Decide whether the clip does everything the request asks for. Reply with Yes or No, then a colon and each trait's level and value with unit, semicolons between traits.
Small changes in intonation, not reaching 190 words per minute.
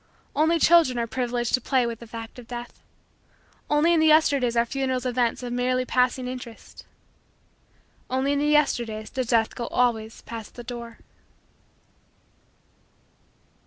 Yes: narrow, 2.2 semitones; average, 145 wpm